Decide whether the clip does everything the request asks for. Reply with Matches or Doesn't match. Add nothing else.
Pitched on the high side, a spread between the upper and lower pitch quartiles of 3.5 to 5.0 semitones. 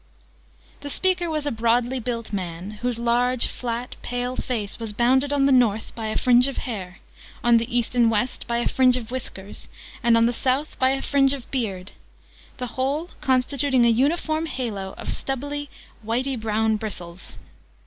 Doesn't match